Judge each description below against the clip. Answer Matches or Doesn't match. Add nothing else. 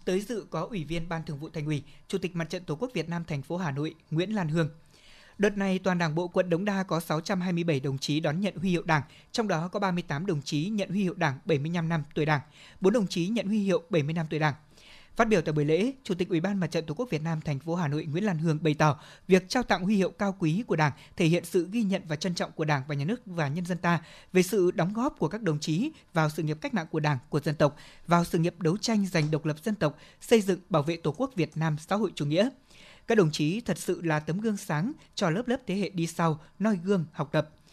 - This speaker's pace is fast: Matches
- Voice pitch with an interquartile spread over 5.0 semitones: Doesn't match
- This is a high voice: Doesn't match